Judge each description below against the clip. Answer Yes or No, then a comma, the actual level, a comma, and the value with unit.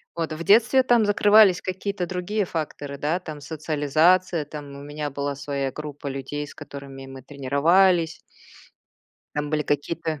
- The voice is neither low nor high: Yes, medium, 155 Hz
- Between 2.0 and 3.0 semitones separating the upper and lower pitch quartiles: No, average, 4.2 semitones